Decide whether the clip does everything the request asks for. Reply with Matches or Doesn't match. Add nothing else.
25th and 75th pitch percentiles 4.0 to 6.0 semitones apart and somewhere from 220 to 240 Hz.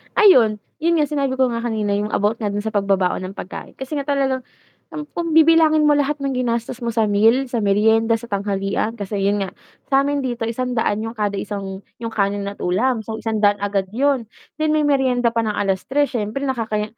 Matches